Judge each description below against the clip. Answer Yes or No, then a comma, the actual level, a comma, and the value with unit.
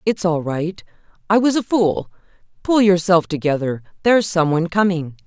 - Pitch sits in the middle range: Yes, medium, 180 Hz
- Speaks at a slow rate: Yes, slow, 125 wpm